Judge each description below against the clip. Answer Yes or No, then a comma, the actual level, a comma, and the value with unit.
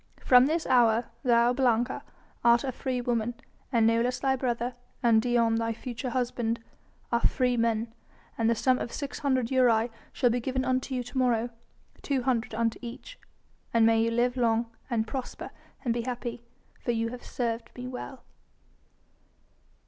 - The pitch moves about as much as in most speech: No, narrow, 1.7 semitones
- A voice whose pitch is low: No, high, 240 Hz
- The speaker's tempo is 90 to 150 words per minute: No, average, 160 wpm